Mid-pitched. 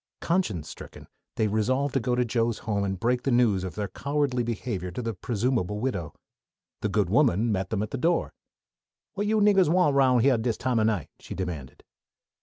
No: low, 115 Hz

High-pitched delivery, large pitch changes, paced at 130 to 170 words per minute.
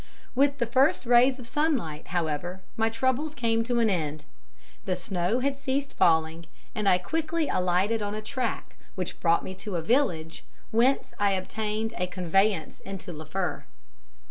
Yes: high, 210 Hz; wide, 6.1 semitones; average, 160 wpm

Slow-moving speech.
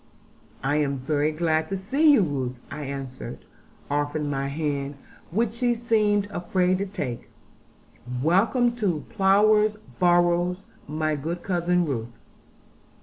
Yes: slow, 130 wpm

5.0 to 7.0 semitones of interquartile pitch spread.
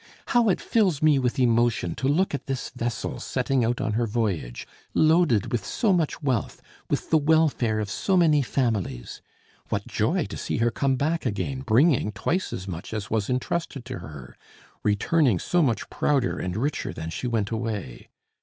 Yes: wide, 5.5 semitones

